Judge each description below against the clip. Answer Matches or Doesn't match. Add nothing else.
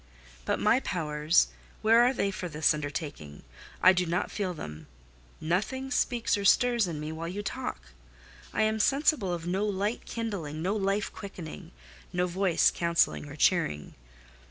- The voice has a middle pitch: Matches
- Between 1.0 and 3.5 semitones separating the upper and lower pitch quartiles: Doesn't match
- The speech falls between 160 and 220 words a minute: Doesn't match